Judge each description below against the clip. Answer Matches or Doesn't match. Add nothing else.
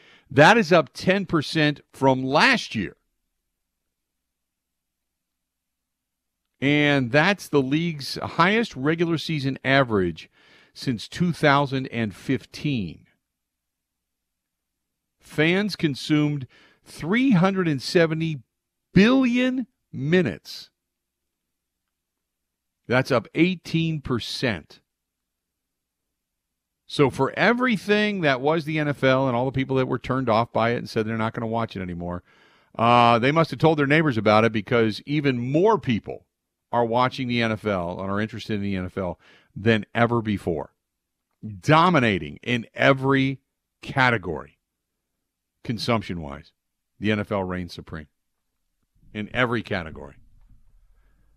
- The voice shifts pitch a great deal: Matches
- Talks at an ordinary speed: Doesn't match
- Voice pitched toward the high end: Doesn't match